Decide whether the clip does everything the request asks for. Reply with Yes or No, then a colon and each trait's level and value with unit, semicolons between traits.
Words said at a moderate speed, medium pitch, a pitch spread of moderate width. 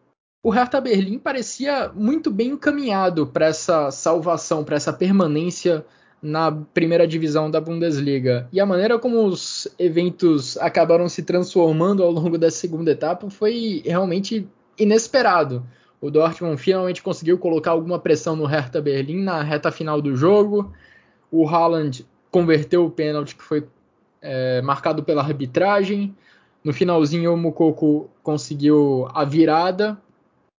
Yes: average, 135 wpm; medium, 170 Hz; average, 3.9 semitones